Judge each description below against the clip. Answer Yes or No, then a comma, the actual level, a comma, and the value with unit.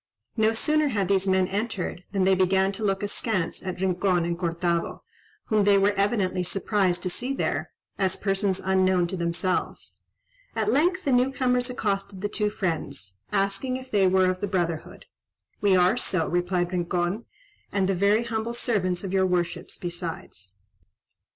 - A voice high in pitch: Yes, high, 195 Hz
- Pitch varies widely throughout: No, average, 2.7 semitones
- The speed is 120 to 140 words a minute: No, average, 165 wpm